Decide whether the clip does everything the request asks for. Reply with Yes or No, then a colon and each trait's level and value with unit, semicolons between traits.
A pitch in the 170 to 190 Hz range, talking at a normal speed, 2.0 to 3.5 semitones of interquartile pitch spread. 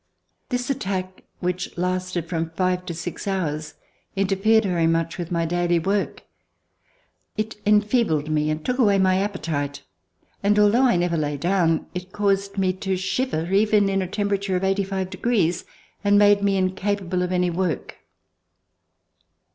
Yes: medium, 185 Hz; average, 155 wpm; average, 2.7 semitones